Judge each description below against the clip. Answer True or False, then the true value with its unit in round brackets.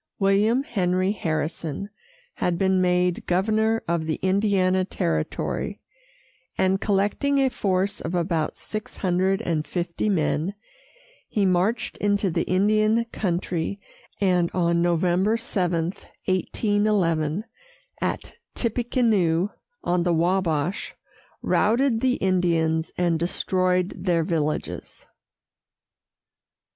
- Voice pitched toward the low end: False (185 Hz)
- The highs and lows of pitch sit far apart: False (3.2 semitones)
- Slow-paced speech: True (100 wpm)